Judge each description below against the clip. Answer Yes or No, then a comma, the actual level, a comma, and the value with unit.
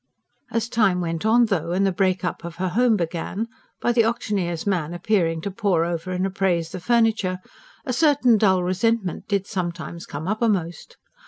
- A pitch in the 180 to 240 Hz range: Yes, high, 190 Hz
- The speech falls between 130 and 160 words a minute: No, average, 175 wpm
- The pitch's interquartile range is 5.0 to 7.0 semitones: No, average, 4.2 semitones